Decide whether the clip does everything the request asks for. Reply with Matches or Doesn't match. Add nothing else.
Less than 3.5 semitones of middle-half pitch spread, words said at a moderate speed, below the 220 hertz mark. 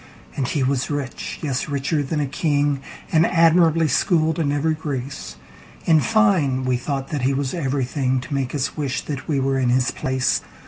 Matches